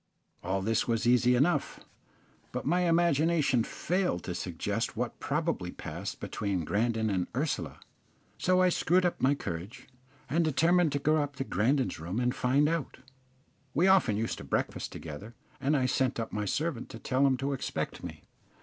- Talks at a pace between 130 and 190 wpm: Yes, average, 170 wpm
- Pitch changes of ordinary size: No, wide, 6.2 semitones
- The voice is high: No, low, 135 Hz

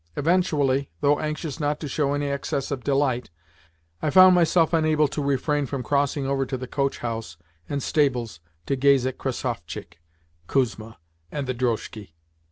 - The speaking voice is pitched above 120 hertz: Yes, medium, 140 Hz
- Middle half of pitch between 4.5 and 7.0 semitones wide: No, narrow, 2.6 semitones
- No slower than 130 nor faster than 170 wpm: Yes, average, 160 wpm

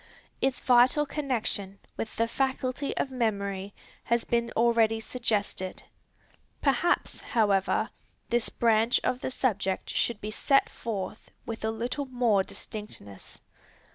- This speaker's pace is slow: Yes, slow, 120 wpm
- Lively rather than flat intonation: No, average, 3.3 semitones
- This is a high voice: Yes, high, 230 Hz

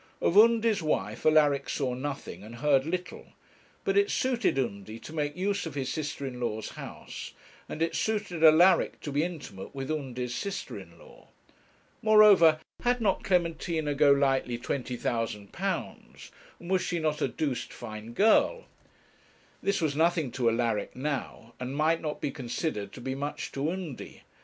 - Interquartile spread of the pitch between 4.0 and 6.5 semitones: Yes, wide, 5.6 semitones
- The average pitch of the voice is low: No, medium, 150 Hz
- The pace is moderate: Yes, average, 155 wpm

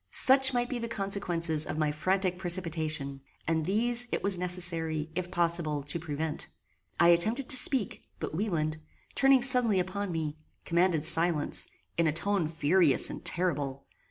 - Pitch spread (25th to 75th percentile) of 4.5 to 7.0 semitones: No, average, 4.1 semitones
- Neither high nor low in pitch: Yes, medium, 175 Hz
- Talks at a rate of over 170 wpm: No, average, 155 wpm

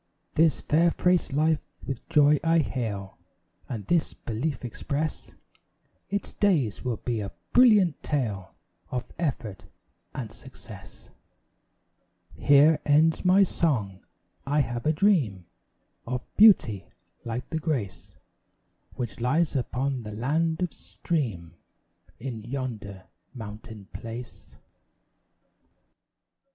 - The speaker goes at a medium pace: No, slow, 105 wpm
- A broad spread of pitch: Yes, wide, 6.2 semitones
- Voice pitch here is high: No, low, 130 Hz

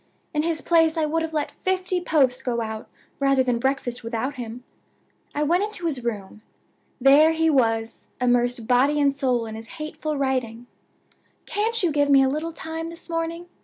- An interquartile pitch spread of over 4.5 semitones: Yes, average, 4.9 semitones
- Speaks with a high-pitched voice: Yes, very high, 280 Hz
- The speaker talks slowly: No, average, 180 wpm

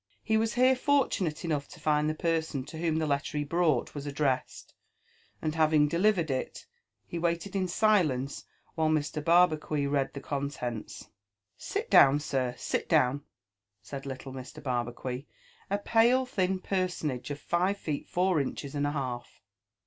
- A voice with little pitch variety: No, average, 4.3 semitones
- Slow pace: No, average, 160 wpm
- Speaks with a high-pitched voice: No, medium, 155 Hz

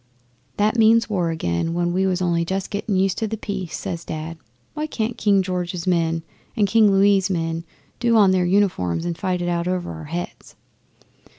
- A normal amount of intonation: Yes, average, 3.3 semitones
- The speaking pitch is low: No, medium, 185 Hz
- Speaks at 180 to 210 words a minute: Yes, average, 190 wpm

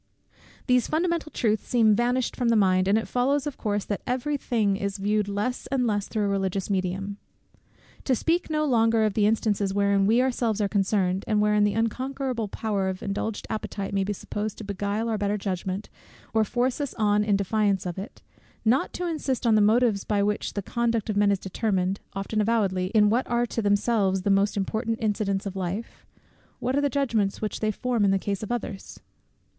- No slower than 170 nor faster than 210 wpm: Yes, average, 200 wpm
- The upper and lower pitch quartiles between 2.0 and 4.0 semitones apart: Yes, average, 3.1 semitones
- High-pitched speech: Yes, high, 210 Hz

